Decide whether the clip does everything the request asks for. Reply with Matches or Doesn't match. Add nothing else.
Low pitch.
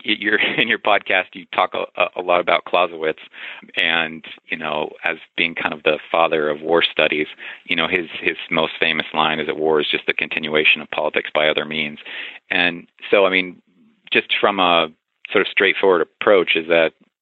Matches